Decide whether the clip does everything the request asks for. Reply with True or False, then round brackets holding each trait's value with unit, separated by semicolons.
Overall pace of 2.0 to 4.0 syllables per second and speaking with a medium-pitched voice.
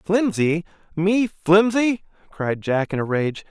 True (3.5 syllables/s; 180 Hz)